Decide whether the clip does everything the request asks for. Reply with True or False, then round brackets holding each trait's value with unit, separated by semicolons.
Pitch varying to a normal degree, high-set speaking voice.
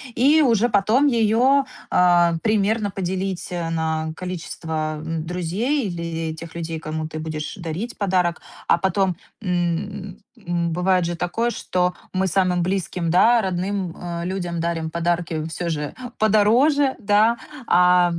False (3.5 semitones; 180 Hz)